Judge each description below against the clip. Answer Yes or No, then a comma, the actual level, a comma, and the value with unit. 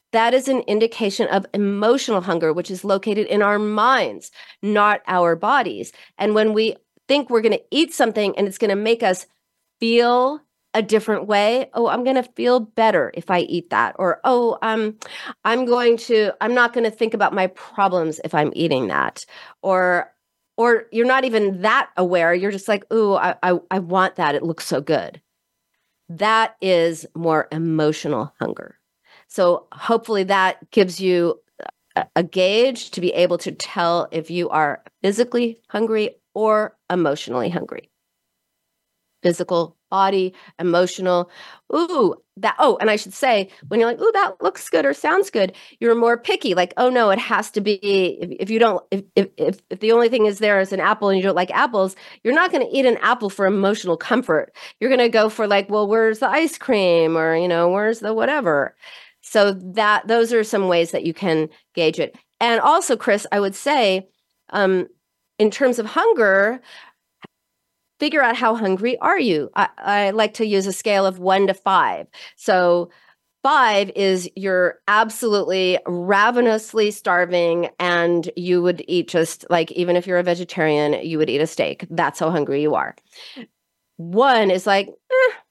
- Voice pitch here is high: Yes, high, 200 Hz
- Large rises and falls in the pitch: No, average, 4.2 semitones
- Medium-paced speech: Yes, average, 180 wpm